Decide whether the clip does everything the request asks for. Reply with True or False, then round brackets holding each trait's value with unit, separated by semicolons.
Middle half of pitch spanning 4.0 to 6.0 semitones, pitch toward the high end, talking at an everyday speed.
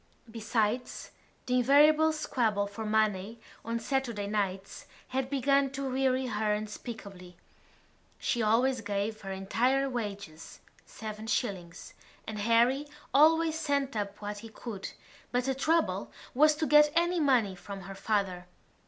False (4.8 semitones; 230 Hz; 125 wpm)